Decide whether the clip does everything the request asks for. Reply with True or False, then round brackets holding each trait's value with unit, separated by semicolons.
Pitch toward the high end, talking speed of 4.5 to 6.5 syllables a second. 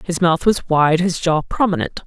False (170 Hz; 4.7 syllables/s)